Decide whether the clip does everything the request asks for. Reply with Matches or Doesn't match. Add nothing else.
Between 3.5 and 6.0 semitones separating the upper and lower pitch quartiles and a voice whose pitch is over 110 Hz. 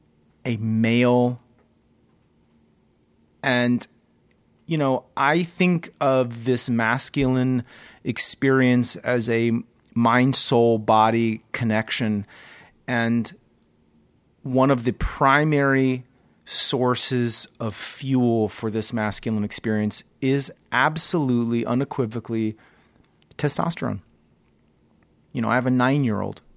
Doesn't match